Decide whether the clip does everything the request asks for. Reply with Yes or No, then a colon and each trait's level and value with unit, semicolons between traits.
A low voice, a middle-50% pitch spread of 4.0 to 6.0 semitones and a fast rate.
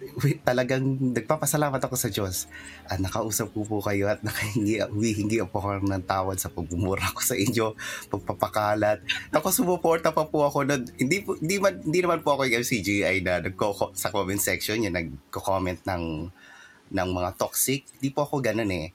Yes: low, 110 Hz; wide, 5.6 semitones; fast, 190 wpm